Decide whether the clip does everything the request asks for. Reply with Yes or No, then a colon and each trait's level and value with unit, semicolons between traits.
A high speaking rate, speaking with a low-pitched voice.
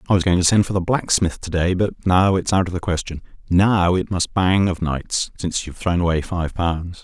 Yes: fast, 245 wpm; very low, 90 Hz